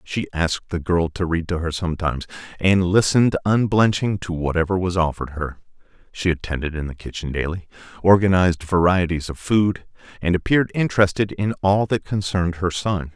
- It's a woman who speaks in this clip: No, male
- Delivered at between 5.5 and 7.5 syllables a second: Yes, 5.6 syllables/s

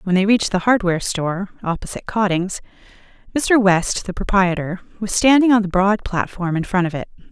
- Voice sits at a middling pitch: No, high, 195 Hz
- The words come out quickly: No, average, 180 wpm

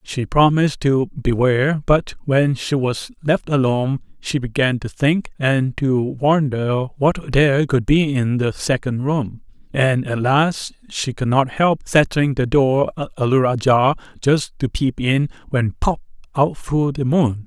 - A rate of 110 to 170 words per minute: Yes, average, 160 wpm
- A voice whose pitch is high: No, low, 135 Hz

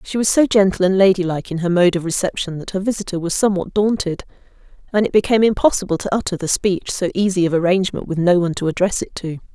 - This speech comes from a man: No, female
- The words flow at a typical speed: No, fast, 225 wpm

